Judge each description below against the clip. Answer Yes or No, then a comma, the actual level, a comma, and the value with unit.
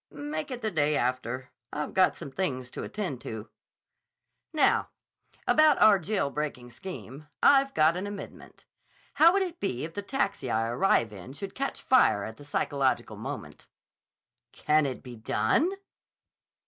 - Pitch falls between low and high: Yes, medium, 155 Hz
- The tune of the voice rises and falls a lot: Yes, wide, 8.3 semitones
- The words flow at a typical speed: Yes, average, 155 wpm